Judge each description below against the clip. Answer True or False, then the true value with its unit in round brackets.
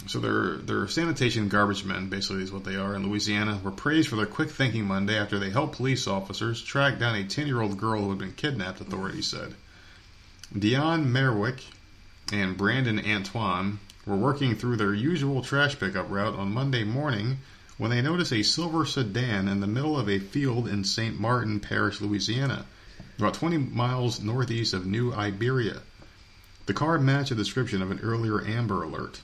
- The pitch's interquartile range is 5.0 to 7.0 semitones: False (4.6 semitones)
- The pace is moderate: True (180 wpm)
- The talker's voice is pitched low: True (105 Hz)